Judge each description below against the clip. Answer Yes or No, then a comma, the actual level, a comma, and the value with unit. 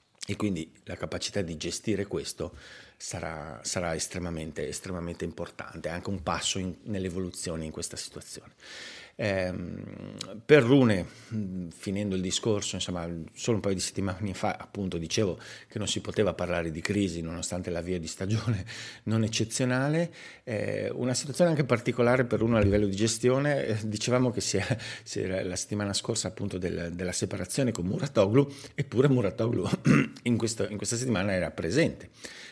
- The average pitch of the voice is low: Yes, low, 100 Hz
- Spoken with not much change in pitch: No, average, 4.3 semitones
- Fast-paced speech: No, average, 160 wpm